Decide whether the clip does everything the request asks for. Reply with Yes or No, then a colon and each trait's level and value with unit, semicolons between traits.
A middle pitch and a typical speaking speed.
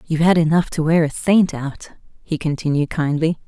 Yes: medium, 160 Hz; average, 190 wpm